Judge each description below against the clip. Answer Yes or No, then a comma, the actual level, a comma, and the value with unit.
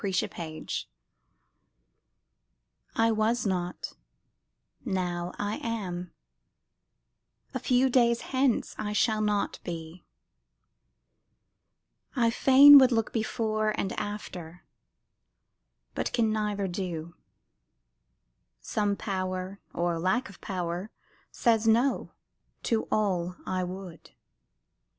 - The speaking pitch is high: Yes, high, 205 Hz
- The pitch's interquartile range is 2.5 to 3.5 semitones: No, average, 4.0 semitones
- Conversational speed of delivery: No, slow, 95 wpm